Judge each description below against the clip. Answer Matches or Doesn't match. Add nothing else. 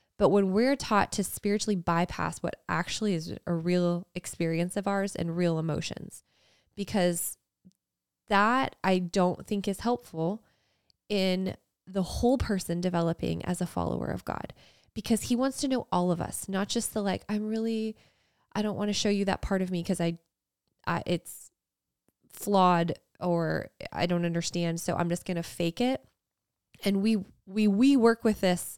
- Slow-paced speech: Doesn't match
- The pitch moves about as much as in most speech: Matches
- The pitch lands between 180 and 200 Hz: Matches